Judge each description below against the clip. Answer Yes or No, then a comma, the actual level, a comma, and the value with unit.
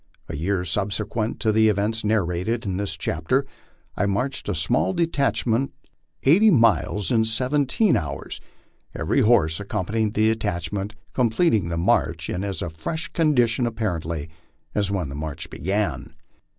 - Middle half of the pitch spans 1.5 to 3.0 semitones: No, average, 4.8 semitones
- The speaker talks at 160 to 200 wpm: No, average, 145 wpm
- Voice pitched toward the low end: Yes, low, 105 Hz